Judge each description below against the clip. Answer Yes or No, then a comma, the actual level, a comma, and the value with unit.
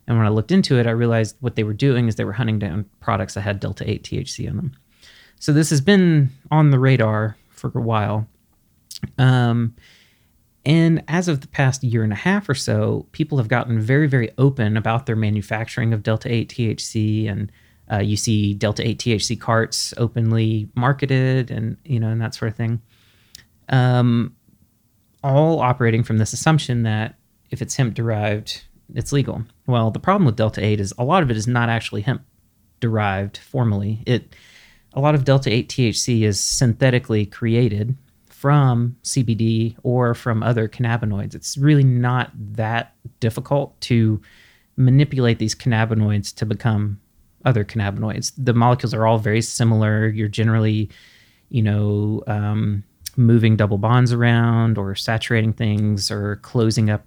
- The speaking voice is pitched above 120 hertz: No, low, 115 Hz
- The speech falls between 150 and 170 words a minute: Yes, average, 165 wpm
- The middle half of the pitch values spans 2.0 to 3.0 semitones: Yes, narrow, 2.6 semitones